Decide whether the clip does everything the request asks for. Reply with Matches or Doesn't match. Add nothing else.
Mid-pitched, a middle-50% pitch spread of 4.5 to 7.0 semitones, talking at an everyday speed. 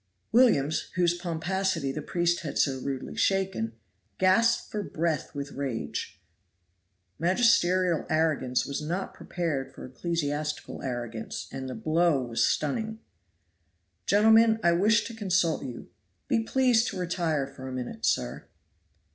Doesn't match